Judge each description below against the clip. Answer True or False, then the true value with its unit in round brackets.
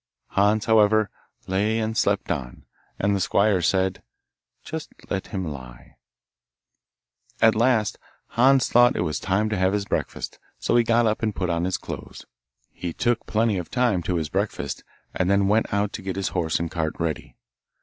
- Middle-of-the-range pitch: False (100 Hz)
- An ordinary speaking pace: True (180 wpm)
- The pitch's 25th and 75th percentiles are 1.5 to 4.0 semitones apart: True (3.6 semitones)